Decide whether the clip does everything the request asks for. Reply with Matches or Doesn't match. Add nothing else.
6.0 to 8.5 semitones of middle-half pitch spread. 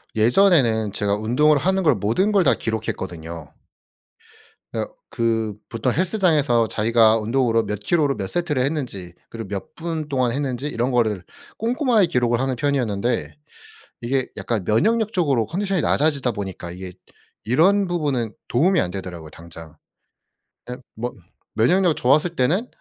Matches